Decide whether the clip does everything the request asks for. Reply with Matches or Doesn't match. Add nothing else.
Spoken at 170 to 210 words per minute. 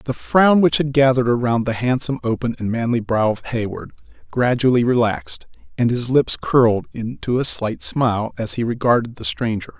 Matches